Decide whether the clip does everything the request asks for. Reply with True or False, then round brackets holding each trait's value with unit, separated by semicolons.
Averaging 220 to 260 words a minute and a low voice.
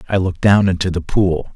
True (230 wpm; 90 Hz)